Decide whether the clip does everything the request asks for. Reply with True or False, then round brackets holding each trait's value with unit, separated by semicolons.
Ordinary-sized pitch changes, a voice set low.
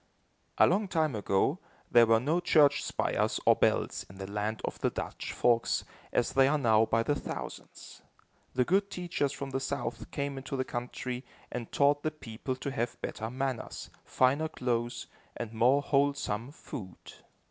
True (3.6 semitones; 130 Hz)